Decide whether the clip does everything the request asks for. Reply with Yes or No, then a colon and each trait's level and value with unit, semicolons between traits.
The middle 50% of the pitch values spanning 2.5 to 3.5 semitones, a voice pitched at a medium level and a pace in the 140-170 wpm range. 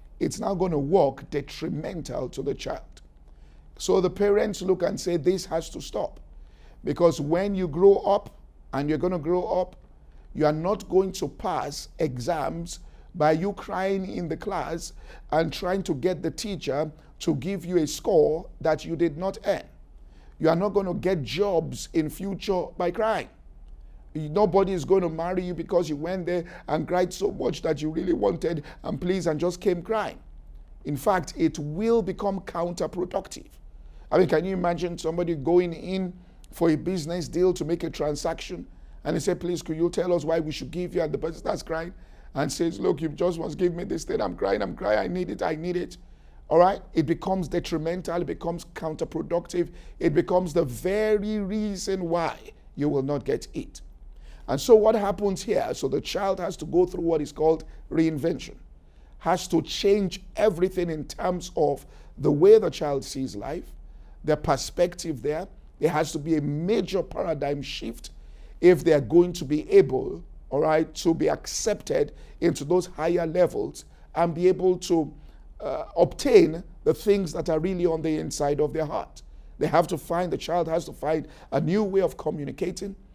No: average, 3.0 semitones; medium, 170 Hz; average, 190 wpm